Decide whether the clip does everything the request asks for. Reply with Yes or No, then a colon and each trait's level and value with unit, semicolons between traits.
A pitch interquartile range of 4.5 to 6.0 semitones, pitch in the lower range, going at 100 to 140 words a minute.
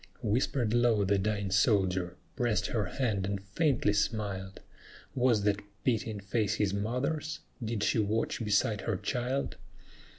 No: average, 3.1 semitones; low, 105 Hz; slow, 135 wpm